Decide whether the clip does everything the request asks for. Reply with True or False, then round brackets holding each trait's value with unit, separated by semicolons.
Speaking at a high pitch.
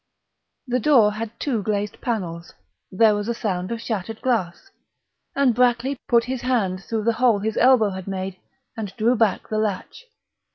True (220 Hz)